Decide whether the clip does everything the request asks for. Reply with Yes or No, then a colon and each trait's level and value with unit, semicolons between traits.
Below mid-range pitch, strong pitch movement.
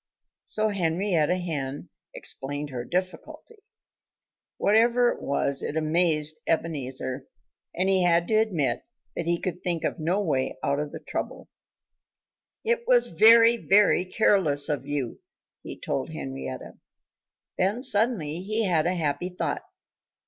No: medium, 170 Hz; wide, 6.0 semitones